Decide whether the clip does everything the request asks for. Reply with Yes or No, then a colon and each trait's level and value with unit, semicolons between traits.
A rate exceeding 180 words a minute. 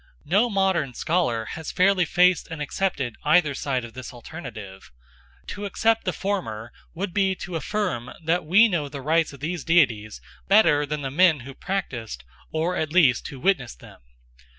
No: average, 170 wpm